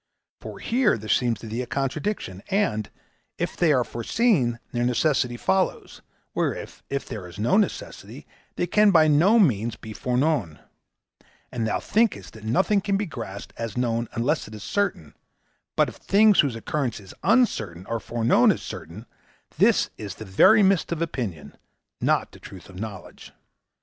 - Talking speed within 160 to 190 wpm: Yes, average, 165 wpm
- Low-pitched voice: Yes, low, 120 Hz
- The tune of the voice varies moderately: No, wide, 8.2 semitones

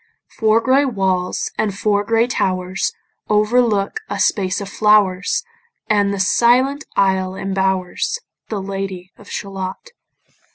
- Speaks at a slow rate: Yes, slow, 120 wpm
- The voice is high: Yes, high, 200 Hz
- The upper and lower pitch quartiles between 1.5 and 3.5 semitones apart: Yes, narrow, 2.4 semitones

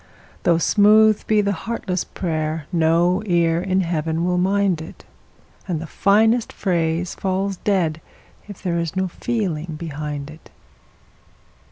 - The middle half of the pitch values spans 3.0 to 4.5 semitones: Yes, average, 3.5 semitones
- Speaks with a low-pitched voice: No, medium, 175 Hz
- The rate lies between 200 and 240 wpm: No, slow, 135 wpm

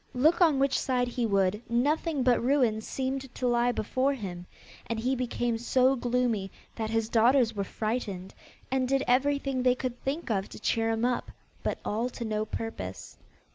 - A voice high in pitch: Yes, high, 245 Hz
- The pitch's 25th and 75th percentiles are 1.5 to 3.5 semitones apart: Yes, average, 2.8 semitones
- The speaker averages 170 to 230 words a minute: Yes, average, 175 wpm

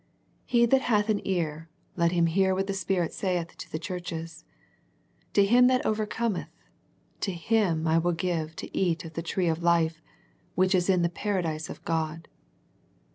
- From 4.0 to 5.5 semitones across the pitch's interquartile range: No, average, 3.2 semitones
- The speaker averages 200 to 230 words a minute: No, average, 175 wpm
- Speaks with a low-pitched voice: No, medium, 175 Hz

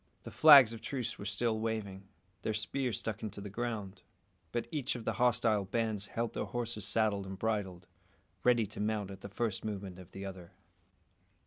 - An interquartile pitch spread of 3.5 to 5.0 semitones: No, average, 2.9 semitones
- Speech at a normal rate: Yes, average, 185 wpm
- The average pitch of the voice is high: No, low, 110 Hz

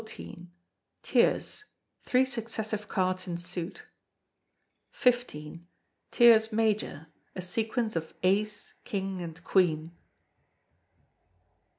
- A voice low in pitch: No, high, 200 Hz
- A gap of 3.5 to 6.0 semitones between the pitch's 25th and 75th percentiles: Yes, average, 4.3 semitones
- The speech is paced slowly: Yes, slow, 80 wpm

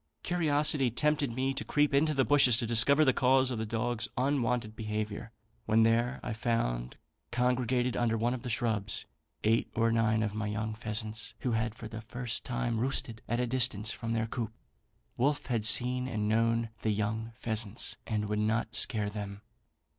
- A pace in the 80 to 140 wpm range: No, average, 180 wpm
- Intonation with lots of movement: No, narrow, 2.5 semitones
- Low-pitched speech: Yes, low, 115 Hz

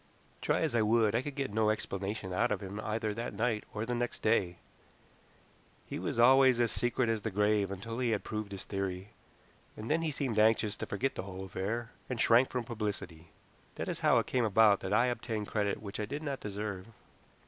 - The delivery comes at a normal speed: No, fast, 210 wpm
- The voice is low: Yes, low, 110 Hz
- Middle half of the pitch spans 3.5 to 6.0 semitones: No, average, 2.9 semitones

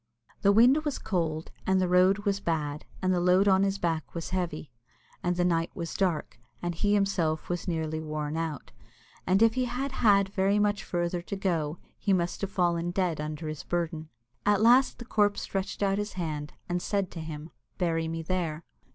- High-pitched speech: No, medium, 180 Hz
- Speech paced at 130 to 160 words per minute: No, average, 195 wpm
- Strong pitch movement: No, average, 3.4 semitones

